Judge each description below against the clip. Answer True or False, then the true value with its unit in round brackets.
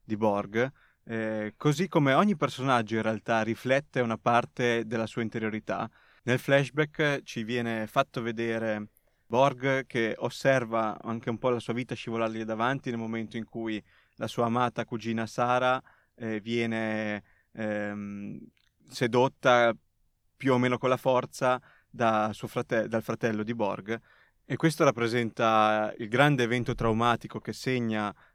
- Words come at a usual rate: True (140 wpm)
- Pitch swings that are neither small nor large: False (2.3 semitones)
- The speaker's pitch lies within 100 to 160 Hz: True (115 Hz)